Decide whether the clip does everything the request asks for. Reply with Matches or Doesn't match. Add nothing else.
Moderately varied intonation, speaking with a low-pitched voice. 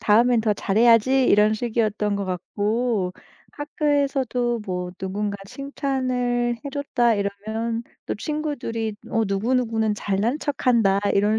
Doesn't match